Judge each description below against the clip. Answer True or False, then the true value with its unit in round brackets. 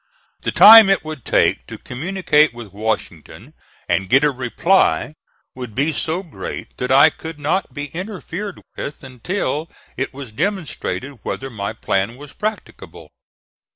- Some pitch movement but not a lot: False (6.1 semitones)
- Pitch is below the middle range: False (145 Hz)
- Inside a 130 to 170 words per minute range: True (145 wpm)